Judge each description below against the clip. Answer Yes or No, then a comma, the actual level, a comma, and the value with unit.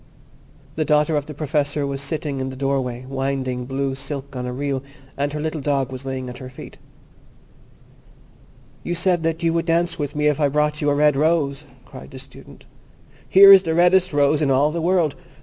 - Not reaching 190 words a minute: No, average, 200 wpm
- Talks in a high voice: No, medium, 145 Hz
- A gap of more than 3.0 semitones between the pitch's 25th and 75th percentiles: No, average, 2.7 semitones